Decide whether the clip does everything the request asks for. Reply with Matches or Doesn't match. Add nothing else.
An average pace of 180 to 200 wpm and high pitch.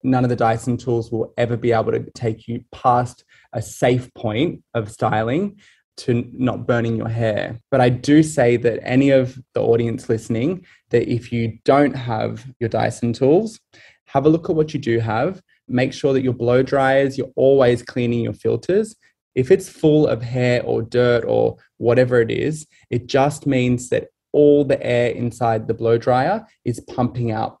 Doesn't match